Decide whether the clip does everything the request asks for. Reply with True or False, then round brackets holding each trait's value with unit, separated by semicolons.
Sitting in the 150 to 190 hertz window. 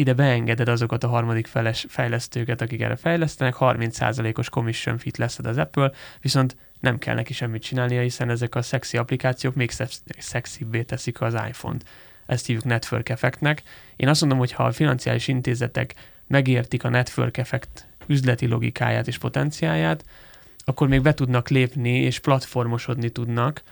False (125 Hz)